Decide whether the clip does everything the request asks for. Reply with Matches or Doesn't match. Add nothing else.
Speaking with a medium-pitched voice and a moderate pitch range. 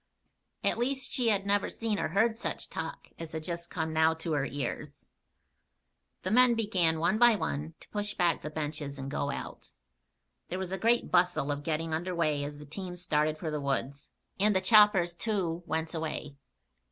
Matches